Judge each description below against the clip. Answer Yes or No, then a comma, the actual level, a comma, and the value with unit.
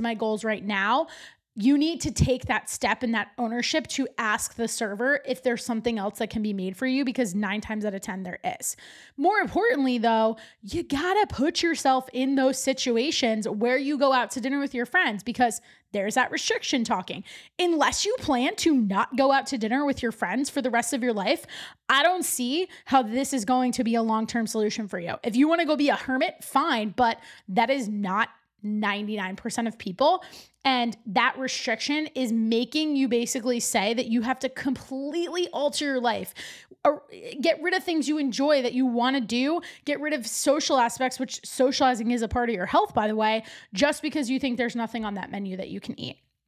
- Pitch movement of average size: Yes, average, 3.9 semitones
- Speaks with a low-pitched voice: No, very high, 255 Hz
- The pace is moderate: No, fast, 215 wpm